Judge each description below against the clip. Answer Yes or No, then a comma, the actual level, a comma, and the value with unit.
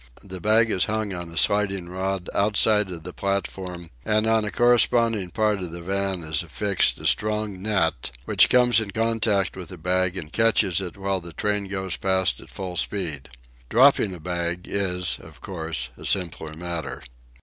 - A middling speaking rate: Yes, average, 180 wpm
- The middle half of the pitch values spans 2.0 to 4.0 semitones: Yes, average, 3.2 semitones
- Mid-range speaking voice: No, very low, 95 Hz